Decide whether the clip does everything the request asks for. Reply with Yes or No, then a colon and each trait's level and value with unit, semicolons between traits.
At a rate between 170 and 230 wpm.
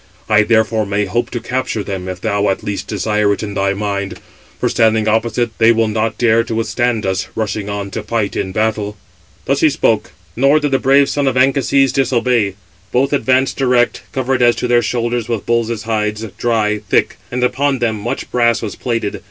Yes: average, 195 wpm